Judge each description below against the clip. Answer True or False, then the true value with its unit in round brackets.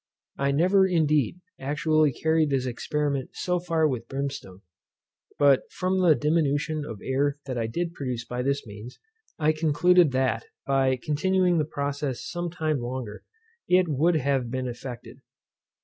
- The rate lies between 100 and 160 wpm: True (150 wpm)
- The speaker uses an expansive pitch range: False (3.7 semitones)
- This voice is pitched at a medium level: True (145 Hz)